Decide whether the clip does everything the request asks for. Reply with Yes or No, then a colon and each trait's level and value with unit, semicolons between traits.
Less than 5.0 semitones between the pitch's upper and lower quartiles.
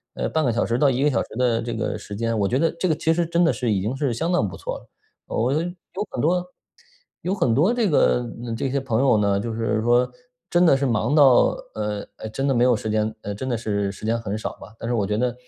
Yes: average, 4.2 semitones